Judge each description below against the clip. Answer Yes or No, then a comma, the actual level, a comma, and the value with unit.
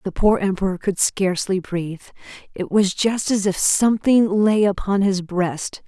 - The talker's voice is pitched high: Yes, high, 195 Hz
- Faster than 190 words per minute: No, average, 165 wpm